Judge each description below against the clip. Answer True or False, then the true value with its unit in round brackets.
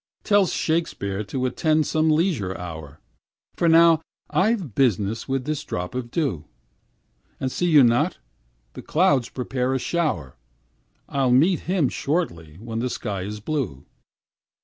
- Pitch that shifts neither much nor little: False (7.4 semitones)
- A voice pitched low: True (130 Hz)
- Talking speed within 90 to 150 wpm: True (140 wpm)